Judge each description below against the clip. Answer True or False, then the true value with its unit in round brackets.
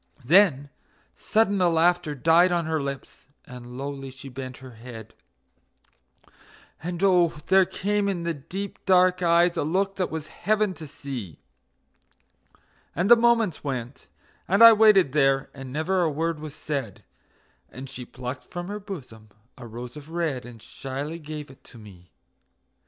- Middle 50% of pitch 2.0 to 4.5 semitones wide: False (5.5 semitones)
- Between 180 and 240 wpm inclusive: False (155 wpm)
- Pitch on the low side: False (155 Hz)